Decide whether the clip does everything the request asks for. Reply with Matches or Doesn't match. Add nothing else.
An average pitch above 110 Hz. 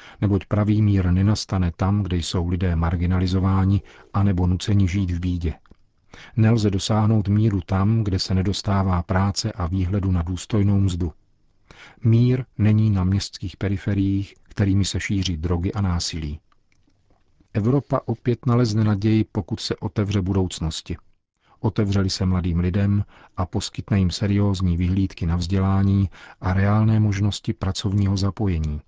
Doesn't match